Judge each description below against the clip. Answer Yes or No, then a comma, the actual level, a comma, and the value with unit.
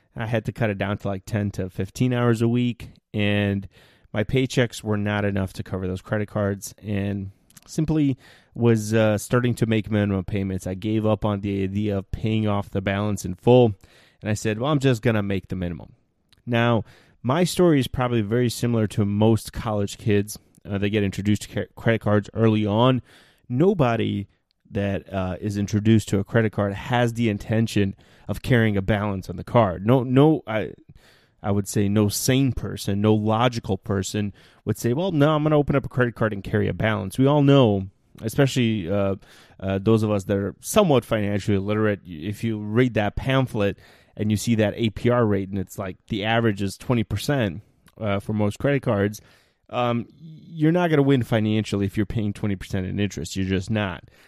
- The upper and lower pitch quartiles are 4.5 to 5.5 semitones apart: No, average, 3.0 semitones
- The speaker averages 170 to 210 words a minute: Yes, fast, 205 wpm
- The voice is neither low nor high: No, low, 105 Hz